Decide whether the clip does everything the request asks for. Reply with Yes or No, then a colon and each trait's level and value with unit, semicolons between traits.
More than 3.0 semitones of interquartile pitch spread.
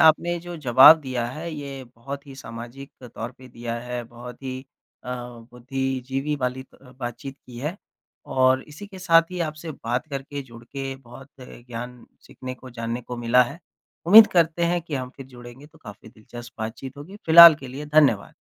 Yes: average, 3.7 semitones